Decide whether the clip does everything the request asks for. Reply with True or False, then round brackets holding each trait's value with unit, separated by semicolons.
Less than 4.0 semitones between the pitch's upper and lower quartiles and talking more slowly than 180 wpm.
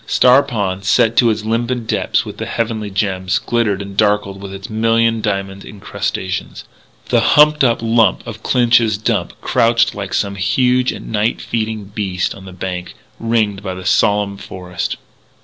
True (2.9 semitones; 165 wpm)